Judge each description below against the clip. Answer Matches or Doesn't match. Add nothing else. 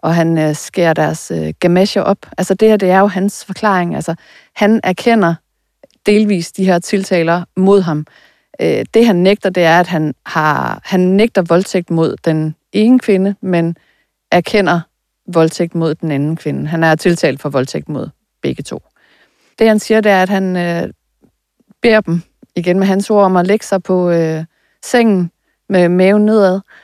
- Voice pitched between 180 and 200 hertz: Matches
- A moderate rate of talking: Matches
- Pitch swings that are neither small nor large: Matches